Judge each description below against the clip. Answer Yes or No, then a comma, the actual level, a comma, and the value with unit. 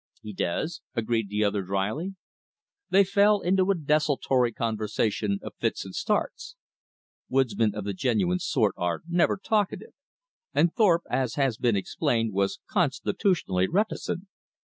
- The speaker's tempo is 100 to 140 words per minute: Yes, slow, 135 wpm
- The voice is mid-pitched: No, low, 125 Hz